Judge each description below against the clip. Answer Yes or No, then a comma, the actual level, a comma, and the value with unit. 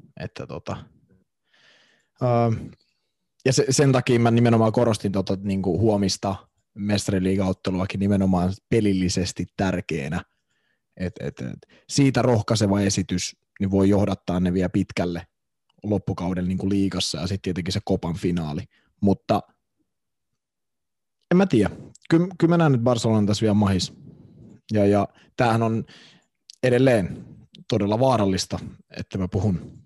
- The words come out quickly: No, average, 125 wpm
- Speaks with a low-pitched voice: Yes, low, 100 Hz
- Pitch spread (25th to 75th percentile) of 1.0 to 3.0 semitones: No, average, 3.7 semitones